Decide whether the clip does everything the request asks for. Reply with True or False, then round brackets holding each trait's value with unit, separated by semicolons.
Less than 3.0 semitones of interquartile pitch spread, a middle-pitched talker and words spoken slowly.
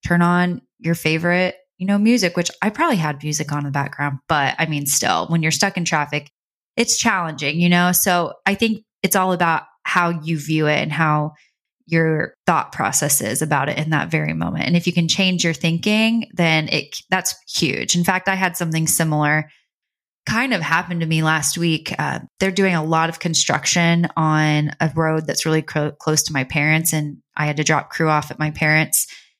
False (2.6 semitones; 165 Hz; 205 wpm)